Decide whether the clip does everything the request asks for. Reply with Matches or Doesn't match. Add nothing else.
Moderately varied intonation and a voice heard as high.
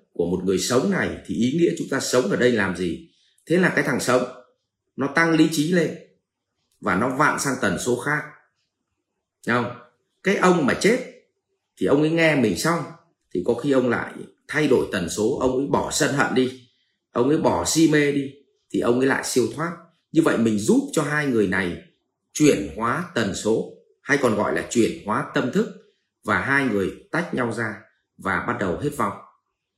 Doesn't match